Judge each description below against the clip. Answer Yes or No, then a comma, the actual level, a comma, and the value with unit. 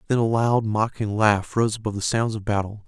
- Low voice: Yes, low, 110 Hz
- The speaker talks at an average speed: No, fast, 230 wpm